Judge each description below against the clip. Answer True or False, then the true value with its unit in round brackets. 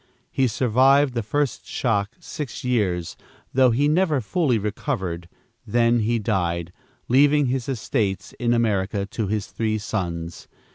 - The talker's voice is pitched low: True (115 Hz)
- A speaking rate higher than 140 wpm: False (135 wpm)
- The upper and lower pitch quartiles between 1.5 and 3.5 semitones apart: False (4.8 semitones)